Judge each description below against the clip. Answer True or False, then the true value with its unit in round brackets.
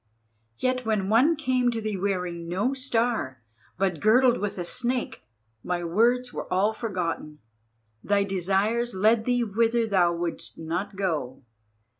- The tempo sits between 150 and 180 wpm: False (140 wpm)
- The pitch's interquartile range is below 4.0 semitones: False (4.9 semitones)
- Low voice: False (205 Hz)